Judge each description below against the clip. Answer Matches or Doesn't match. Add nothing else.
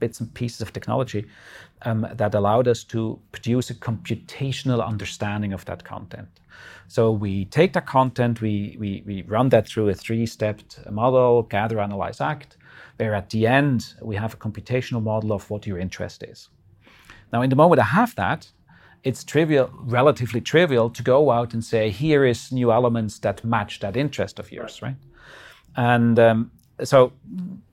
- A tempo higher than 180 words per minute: Doesn't match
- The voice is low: Matches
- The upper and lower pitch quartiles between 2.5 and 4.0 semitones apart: Matches